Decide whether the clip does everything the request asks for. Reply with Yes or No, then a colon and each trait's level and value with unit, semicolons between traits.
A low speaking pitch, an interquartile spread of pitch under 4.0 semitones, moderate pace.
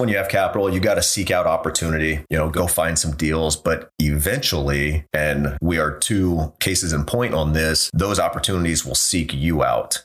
Yes: very low, 80 Hz; narrow, 2.4 semitones; average, 195 wpm